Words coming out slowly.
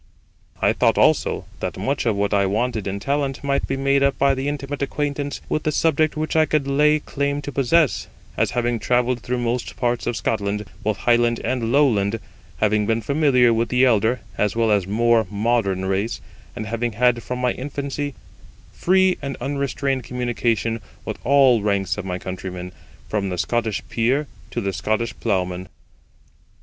No: average, 175 wpm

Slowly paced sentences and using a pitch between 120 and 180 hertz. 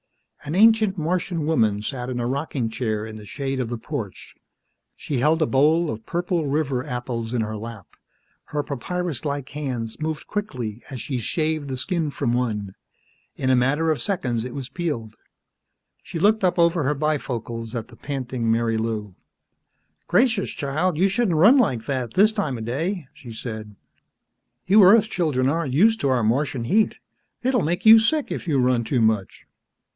No: average, 175 wpm; medium, 140 Hz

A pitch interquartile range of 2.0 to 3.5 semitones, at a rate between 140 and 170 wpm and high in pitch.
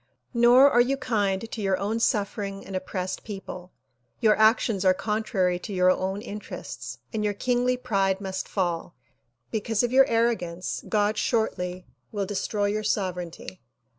Yes: average, 3.2 semitones; average, 150 wpm; high, 205 Hz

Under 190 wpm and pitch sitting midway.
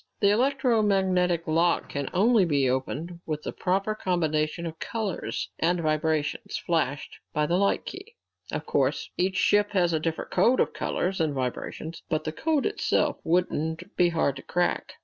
Yes: average, 165 wpm; medium, 175 Hz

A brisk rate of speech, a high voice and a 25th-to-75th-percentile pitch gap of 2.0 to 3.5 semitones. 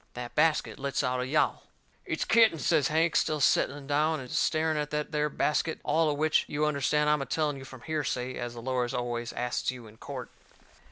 No: fast, 215 wpm; medium, 145 Hz; average, 3.2 semitones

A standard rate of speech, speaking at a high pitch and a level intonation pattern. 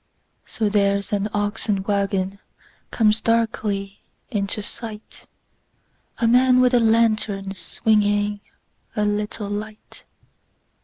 No: slow, 85 wpm; high, 210 Hz; narrow, 1.8 semitones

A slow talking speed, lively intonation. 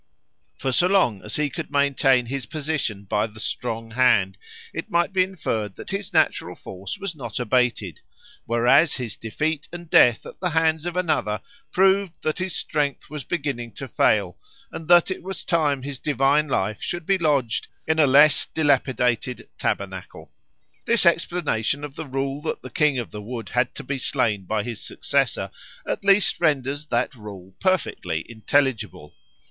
No: average, 170 wpm; wide, 5.8 semitones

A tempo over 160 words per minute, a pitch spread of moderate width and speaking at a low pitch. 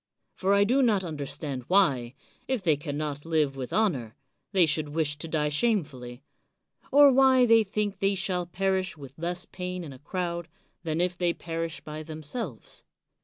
No: average, 175 wpm; average, 4.8 semitones; medium, 170 Hz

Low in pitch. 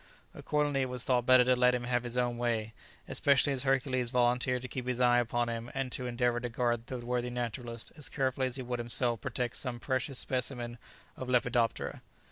Yes: low, 125 Hz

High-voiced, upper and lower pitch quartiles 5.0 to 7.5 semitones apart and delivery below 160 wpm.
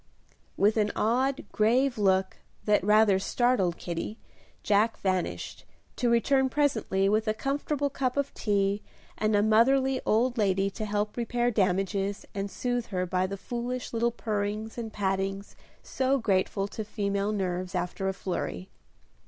No: high, 210 Hz; average, 3.6 semitones; average, 145 wpm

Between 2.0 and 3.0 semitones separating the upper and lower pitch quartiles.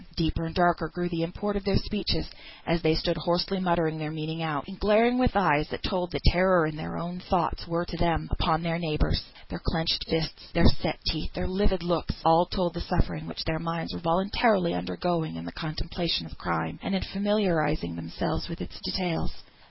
Yes: narrow, 2.5 semitones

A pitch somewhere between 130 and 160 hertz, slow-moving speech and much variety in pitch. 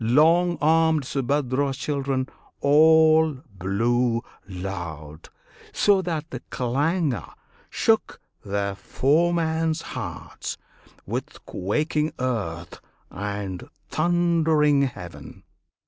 Yes: medium, 140 Hz; slow, 80 wpm; wide, 7.6 semitones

